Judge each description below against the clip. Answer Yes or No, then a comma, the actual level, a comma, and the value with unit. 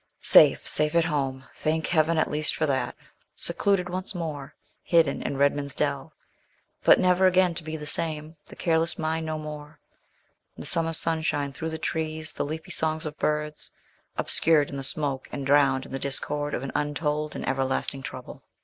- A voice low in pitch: No, medium, 155 Hz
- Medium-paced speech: Yes, average, 175 wpm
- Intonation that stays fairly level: Yes, narrow, 2.1 semitones